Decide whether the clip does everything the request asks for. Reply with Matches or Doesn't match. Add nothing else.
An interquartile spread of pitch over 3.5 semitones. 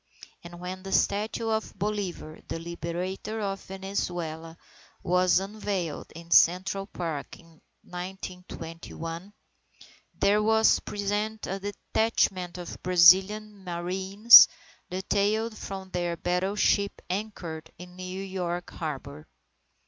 Doesn't match